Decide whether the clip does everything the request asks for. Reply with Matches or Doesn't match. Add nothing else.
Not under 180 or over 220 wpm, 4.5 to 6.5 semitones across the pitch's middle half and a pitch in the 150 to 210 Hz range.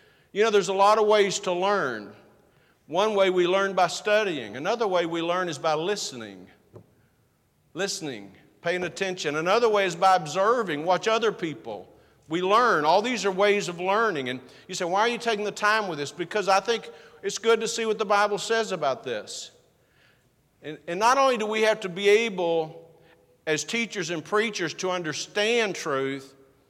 Matches